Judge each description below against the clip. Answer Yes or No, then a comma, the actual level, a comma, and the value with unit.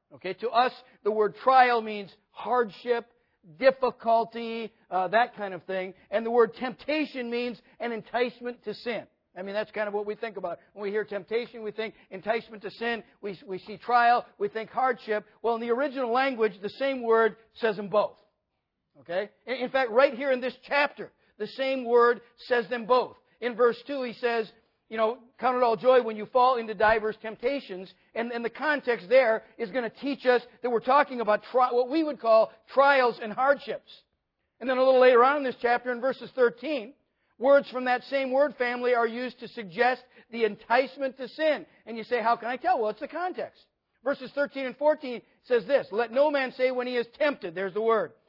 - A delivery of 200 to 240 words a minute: Yes, fast, 205 wpm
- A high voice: Yes, high, 240 Hz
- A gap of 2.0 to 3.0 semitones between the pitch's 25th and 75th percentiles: Yes, average, 2.7 semitones